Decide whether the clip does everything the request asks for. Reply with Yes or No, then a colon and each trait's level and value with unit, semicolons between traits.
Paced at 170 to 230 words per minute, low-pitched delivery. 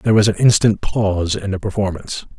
Yes: average, 200 wpm; low, 100 Hz